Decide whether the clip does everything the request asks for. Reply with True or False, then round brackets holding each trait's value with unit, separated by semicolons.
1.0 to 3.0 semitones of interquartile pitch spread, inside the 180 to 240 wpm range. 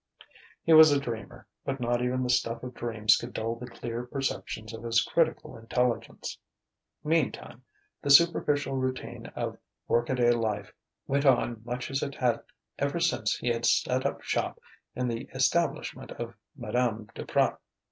False (2.5 semitones; 160 wpm)